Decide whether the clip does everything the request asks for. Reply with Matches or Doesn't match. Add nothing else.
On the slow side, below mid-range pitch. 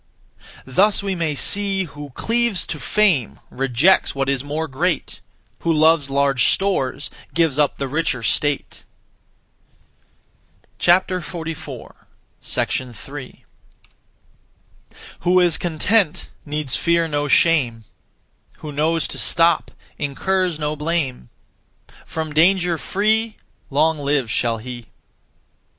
Doesn't match